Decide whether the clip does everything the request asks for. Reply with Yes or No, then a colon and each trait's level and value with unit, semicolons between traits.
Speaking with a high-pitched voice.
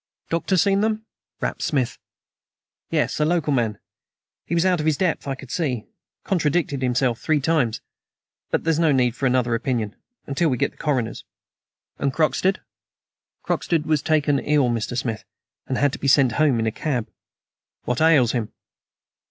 No: medium, 140 Hz